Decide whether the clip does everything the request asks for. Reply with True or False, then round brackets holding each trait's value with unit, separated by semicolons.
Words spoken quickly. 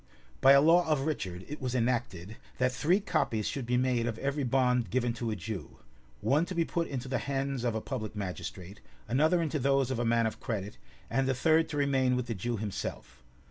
True (220 wpm)